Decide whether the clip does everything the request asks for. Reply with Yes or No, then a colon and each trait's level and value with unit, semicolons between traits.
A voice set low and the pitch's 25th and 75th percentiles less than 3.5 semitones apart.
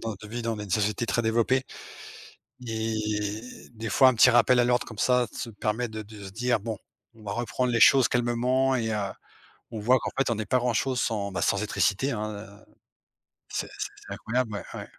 Yes: low, 115 Hz; narrow, 2.4 semitones